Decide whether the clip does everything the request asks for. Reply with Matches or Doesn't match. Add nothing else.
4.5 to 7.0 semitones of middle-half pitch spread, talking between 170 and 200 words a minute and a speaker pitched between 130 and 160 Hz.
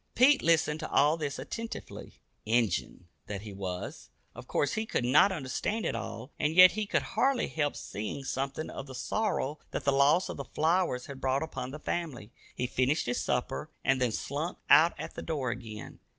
Matches